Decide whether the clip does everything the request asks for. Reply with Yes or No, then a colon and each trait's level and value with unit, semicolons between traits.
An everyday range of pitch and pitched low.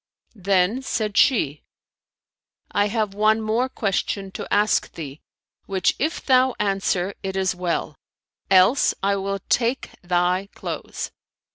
No: average, 3.0 semitones; high, 200 Hz